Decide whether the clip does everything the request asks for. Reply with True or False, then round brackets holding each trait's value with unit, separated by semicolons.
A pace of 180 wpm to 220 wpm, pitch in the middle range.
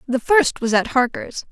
False (200 wpm; 265 Hz)